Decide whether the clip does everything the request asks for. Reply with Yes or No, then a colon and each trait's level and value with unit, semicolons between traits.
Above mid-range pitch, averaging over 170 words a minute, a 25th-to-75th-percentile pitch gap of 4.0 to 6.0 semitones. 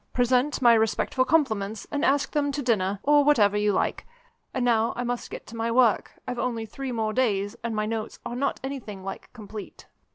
No: high, 235 Hz; average, 200 wpm; average, 3.3 semitones